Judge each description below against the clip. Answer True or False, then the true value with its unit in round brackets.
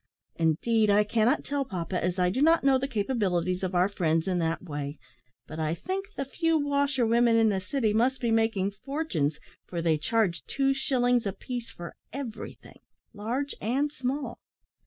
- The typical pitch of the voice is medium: False (225 Hz)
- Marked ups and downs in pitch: True (6.9 semitones)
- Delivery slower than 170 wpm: False (175 wpm)